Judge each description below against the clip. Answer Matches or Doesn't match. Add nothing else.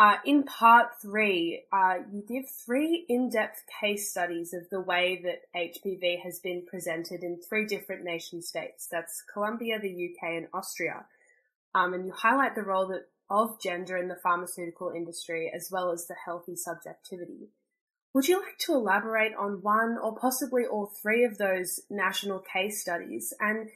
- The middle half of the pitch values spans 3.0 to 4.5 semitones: Matches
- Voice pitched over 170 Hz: Matches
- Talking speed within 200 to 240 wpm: Doesn't match